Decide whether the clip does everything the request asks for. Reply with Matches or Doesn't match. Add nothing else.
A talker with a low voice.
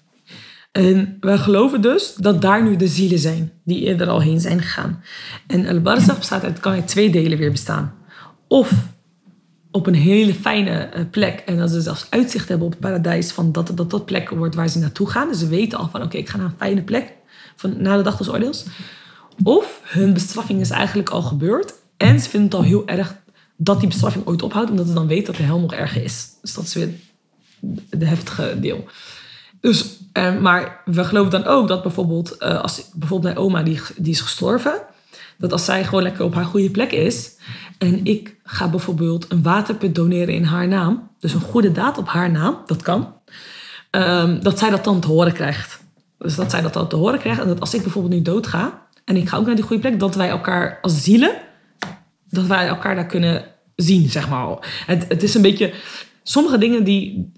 Doesn't match